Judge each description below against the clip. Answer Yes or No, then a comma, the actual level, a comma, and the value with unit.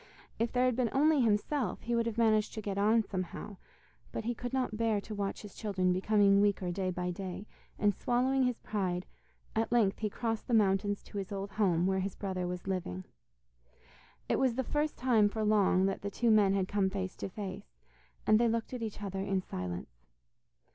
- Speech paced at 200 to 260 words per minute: Yes, fast, 205 wpm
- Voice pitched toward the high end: Yes, high, 205 Hz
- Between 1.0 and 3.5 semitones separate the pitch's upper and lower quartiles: Yes, average, 3.2 semitones